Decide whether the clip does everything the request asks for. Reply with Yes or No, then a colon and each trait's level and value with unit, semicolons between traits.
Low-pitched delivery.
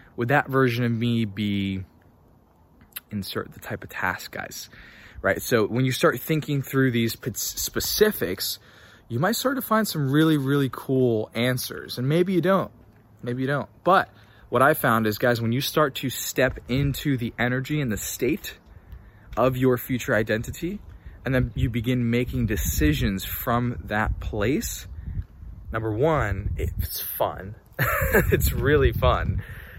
Yes: low, 120 Hz